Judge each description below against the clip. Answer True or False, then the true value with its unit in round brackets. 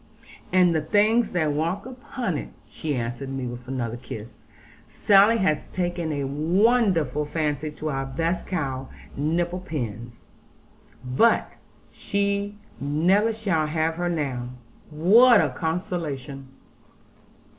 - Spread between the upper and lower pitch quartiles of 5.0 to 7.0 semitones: True (5.6 semitones)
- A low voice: False (160 Hz)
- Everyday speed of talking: False (120 wpm)